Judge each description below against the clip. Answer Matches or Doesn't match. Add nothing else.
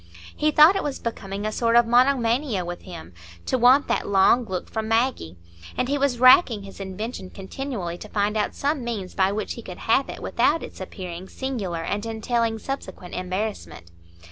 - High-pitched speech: Matches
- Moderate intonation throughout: Matches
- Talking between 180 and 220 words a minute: Matches